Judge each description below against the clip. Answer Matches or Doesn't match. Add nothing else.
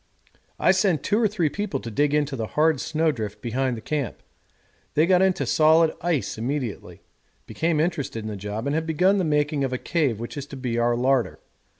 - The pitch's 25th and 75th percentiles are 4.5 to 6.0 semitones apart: Matches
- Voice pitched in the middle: Matches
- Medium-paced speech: Doesn't match